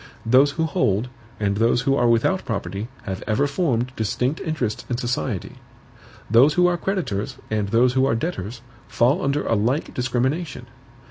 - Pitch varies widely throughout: No, average, 4.2 semitones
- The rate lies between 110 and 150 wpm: No, average, 160 wpm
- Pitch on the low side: Yes, low, 125 Hz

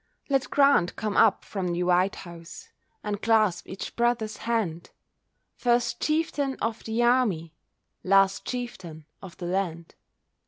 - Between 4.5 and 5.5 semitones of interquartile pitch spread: Yes, average, 5.2 semitones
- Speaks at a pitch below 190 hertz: No, high, 205 Hz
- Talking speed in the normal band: No, slow, 130 wpm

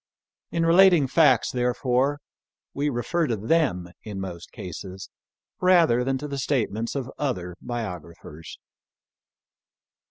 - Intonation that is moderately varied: No, wide, 7.3 semitones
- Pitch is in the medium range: No, low, 125 Hz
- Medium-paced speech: No, slow, 115 wpm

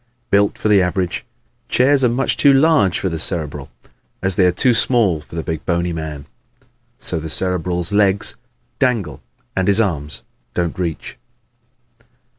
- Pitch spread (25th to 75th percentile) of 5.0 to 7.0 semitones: No, average, 4.2 semitones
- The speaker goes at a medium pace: Yes, average, 160 wpm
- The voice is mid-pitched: No, very low, 90 Hz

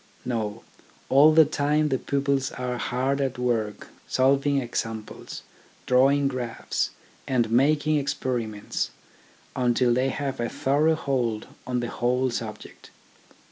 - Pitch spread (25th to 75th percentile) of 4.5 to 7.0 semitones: No, narrow, 2.6 semitones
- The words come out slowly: Yes, slow, 120 wpm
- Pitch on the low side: Yes, low, 130 Hz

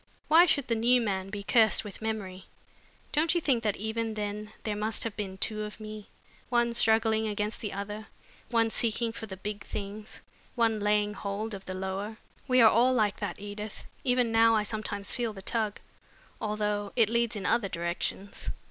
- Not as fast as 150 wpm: No, average, 185 wpm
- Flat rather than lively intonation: Yes, narrow, 1.9 semitones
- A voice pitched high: Yes, high, 215 Hz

